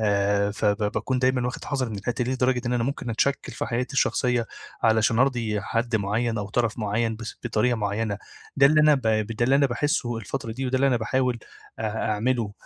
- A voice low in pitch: Yes, low, 120 Hz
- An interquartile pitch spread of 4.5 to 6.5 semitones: No, average, 2.9 semitones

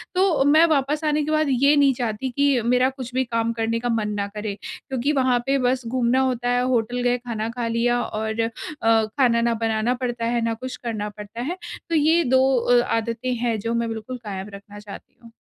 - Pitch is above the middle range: Yes, high, 240 Hz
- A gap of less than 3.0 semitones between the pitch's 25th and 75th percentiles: Yes, narrow, 2.5 semitones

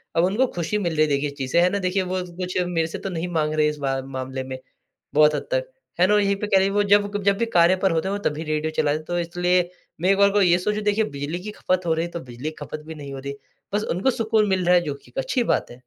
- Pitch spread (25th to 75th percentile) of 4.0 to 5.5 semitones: Yes, average, 4.5 semitones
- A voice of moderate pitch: Yes, medium, 175 Hz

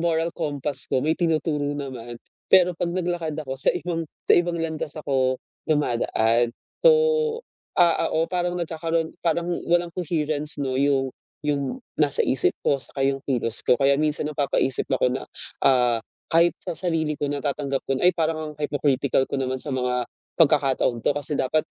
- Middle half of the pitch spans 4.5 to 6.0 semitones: No, average, 3.5 semitones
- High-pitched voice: No, medium, 150 Hz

